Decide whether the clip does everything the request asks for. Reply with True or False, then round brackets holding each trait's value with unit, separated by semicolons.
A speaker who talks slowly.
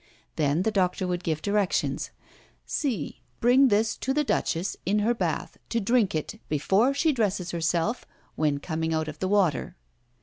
False (165 wpm)